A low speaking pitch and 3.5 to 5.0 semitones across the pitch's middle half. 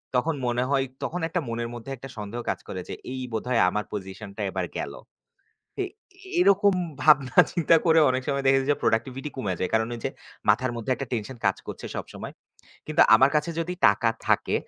Yes: low, 125 Hz; average, 4.4 semitones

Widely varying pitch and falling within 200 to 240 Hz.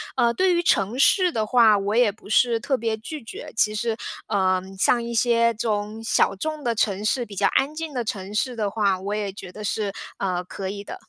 No: average, 3.0 semitones; high, 220 Hz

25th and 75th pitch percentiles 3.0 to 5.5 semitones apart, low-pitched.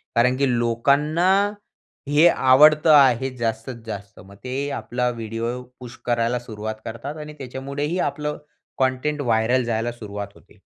Yes: average, 3.5 semitones; low, 125 Hz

